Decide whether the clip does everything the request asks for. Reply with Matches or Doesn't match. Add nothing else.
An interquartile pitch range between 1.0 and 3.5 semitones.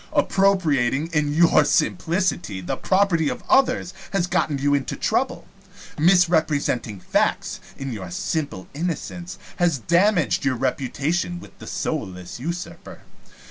Doesn't match